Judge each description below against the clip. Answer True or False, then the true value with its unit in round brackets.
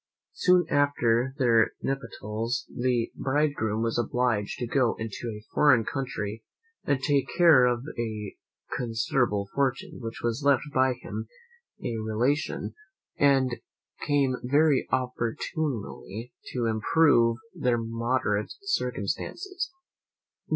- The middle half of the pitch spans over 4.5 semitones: False (3.5 semitones)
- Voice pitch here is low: True (125 Hz)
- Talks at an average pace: False (110 wpm)